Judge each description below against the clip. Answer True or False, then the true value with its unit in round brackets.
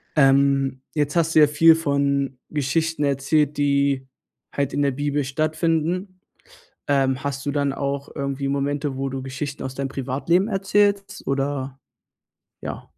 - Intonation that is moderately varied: False (2.2 semitones)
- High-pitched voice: False (140 Hz)